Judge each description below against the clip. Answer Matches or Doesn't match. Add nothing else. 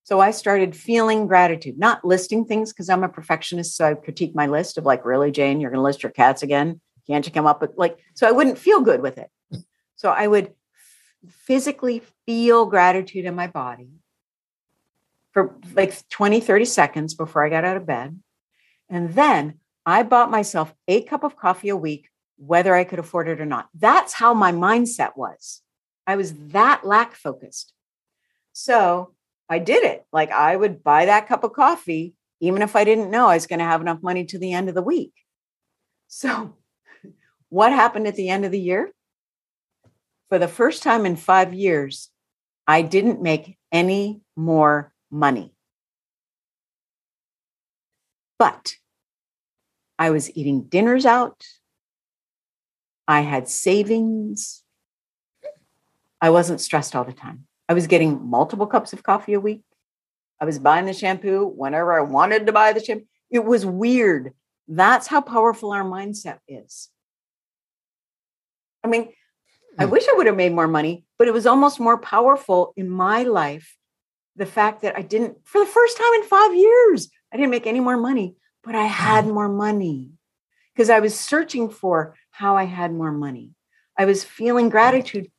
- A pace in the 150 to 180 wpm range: Matches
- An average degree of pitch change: Doesn't match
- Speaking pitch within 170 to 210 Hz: Matches